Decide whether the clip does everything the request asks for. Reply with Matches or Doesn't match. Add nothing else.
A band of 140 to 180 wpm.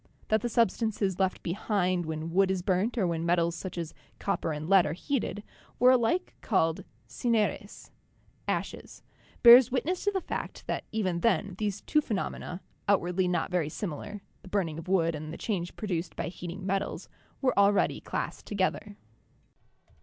Matches